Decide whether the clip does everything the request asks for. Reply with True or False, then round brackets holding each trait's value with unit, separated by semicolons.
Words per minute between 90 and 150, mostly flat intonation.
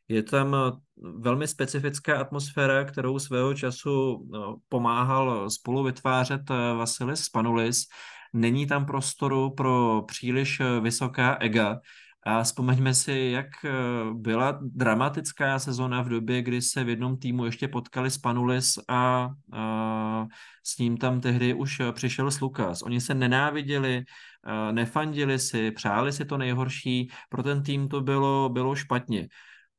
True (125 wpm; 2.2 semitones)